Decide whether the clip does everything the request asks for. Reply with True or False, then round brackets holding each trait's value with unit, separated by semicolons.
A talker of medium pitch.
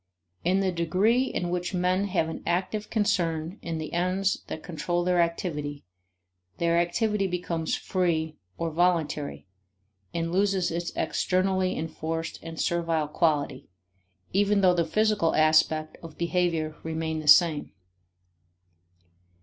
True (170 Hz)